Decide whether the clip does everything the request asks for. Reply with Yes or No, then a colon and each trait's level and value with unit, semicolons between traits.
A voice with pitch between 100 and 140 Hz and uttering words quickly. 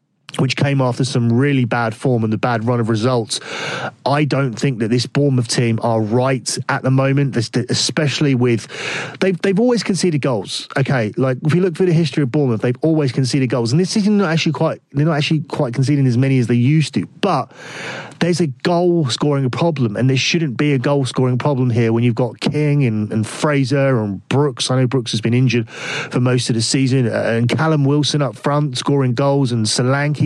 Yes: low, 135 Hz; fast, 215 wpm